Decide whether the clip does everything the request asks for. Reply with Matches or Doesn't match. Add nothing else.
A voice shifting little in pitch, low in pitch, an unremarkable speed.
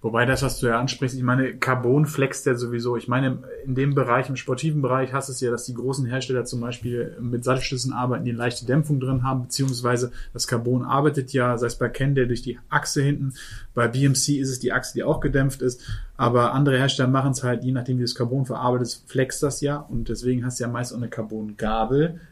Doesn't match